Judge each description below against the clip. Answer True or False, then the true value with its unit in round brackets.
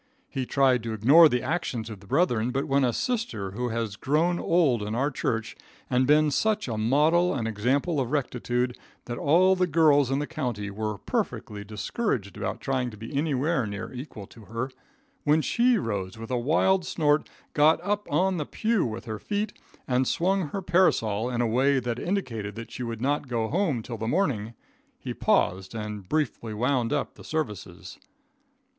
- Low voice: True (125 Hz)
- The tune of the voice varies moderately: False (5.8 semitones)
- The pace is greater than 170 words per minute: True (185 wpm)